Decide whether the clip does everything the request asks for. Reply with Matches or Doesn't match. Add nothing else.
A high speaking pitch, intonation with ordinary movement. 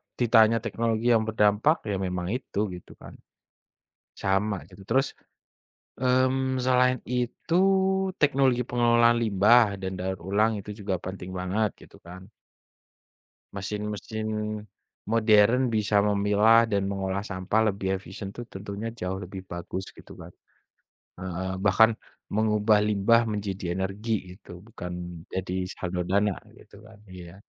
Doesn't match